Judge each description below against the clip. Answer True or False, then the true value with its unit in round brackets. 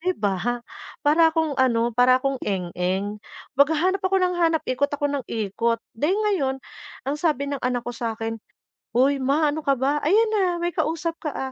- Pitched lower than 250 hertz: False (280 Hz)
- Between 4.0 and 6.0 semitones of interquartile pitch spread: True (5.2 semitones)